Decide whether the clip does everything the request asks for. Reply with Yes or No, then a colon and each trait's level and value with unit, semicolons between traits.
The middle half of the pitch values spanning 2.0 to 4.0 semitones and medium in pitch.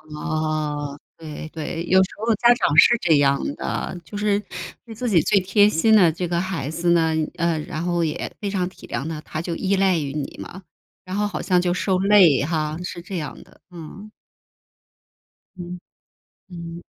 Yes: average, 3.5 semitones; medium, 175 Hz